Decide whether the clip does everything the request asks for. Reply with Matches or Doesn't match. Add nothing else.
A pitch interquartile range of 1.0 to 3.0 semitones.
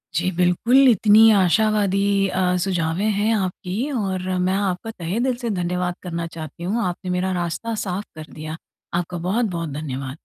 Doesn't match